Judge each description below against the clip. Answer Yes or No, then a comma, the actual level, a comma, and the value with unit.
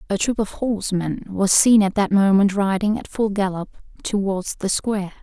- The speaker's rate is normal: Yes, average, 185 wpm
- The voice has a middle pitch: No, high, 200 Hz